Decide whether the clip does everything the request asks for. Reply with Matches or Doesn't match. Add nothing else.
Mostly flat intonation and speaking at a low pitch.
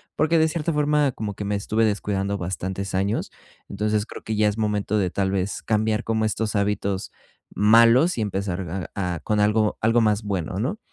Matches